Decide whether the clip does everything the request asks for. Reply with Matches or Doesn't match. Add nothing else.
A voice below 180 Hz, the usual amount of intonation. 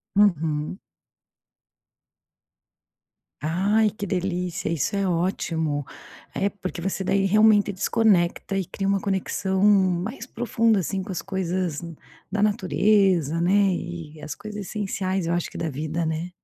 Doesn't match